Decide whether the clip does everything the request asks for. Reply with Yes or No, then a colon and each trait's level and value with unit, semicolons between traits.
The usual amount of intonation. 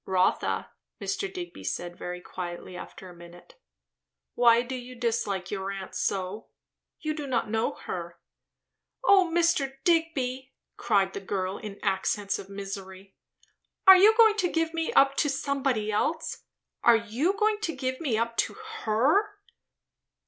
No: wide, 8.8 semitones